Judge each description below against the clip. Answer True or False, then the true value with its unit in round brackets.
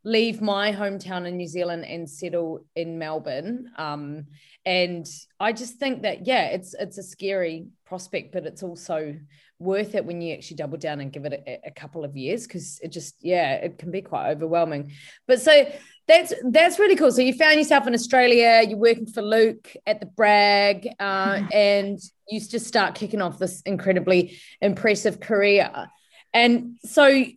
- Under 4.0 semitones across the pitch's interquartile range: False (5.0 semitones)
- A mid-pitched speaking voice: False (195 Hz)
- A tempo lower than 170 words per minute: False (180 wpm)